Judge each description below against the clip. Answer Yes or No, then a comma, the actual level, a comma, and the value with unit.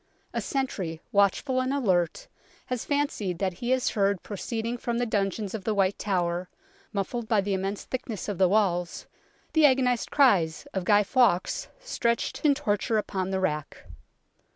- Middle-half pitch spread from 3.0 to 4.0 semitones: No, average, 4.6 semitones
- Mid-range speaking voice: No, high, 205 Hz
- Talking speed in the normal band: Yes, average, 165 wpm